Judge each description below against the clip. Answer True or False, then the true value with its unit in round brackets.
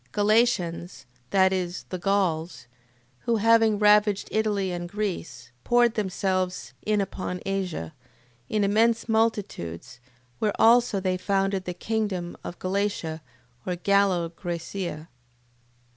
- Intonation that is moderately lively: True (3.1 semitones)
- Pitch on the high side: True (195 Hz)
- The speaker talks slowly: True (115 wpm)